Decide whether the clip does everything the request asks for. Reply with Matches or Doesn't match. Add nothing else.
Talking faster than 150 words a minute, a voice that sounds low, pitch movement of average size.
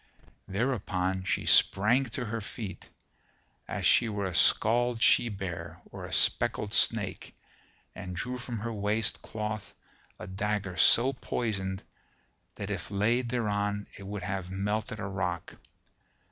Doesn't match